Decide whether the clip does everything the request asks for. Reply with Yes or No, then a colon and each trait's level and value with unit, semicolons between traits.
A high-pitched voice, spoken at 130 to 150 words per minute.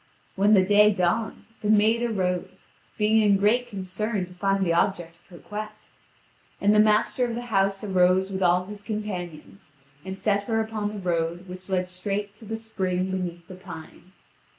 No: high, 195 Hz; average, 180 wpm